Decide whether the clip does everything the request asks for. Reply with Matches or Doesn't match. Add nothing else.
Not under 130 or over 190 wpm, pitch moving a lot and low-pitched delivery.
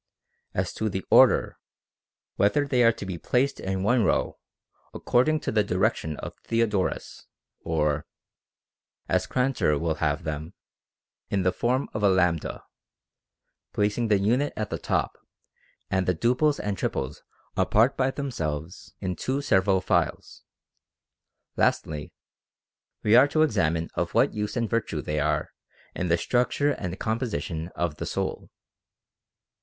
Matches